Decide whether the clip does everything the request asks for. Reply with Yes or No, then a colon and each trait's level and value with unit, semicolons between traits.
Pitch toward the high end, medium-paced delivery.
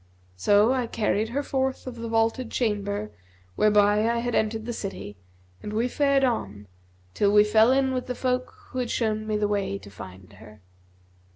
Yes: high, 220 Hz; average, 185 wpm